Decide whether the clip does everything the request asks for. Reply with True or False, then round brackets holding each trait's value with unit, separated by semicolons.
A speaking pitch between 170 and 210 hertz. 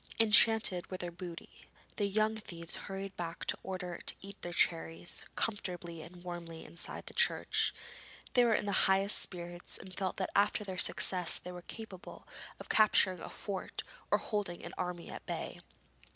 True (185 Hz)